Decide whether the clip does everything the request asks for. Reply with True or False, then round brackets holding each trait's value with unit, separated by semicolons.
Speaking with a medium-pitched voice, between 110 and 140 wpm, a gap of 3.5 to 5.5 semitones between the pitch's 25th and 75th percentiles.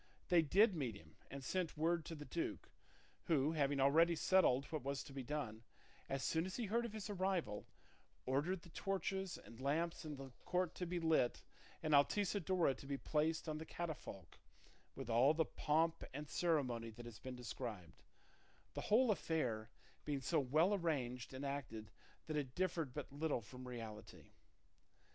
False (150 Hz; 170 wpm; 4.9 semitones)